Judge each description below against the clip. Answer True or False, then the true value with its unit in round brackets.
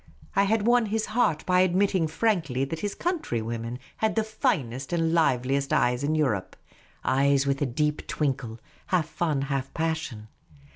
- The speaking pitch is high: False (155 Hz)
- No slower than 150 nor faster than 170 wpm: True (160 wpm)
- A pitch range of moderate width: False (6.0 semitones)